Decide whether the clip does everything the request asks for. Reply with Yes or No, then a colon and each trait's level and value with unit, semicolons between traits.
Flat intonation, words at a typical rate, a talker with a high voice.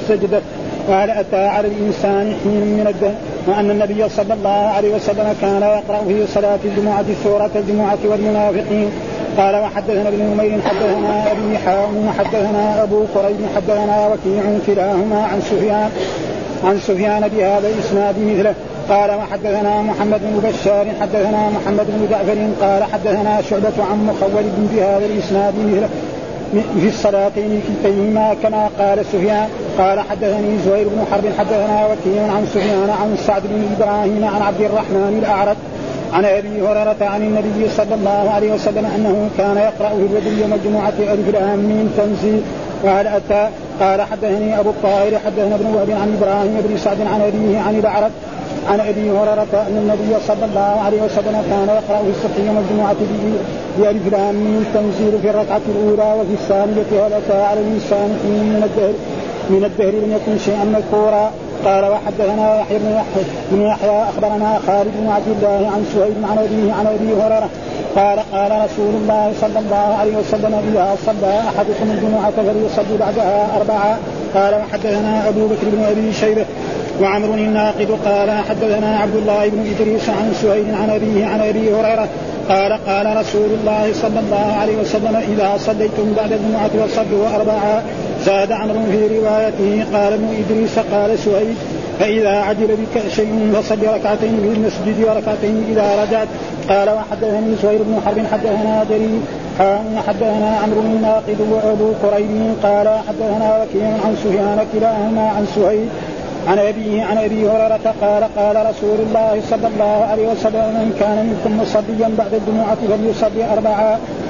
No: narrow, 0.9 semitones; fast, 150 wpm; high, 210 Hz